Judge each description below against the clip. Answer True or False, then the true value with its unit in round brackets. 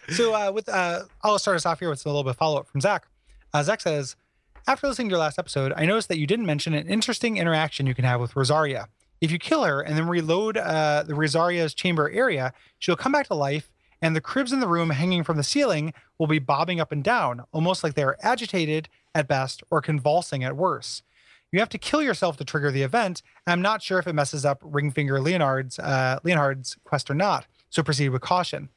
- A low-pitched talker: False (155 Hz)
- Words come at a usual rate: False (235 wpm)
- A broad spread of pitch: False (4.0 semitones)